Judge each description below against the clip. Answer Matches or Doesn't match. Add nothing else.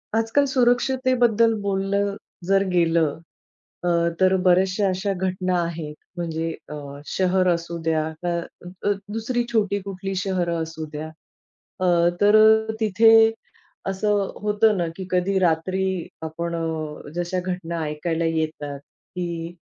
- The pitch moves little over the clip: Doesn't match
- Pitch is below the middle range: Doesn't match